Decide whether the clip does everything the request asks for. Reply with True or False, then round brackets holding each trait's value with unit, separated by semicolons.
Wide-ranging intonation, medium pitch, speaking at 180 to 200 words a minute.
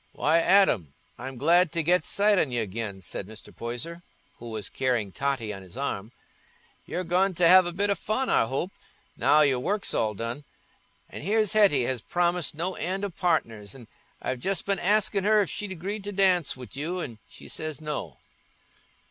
True (7.8 semitones; 160 Hz; 190 wpm)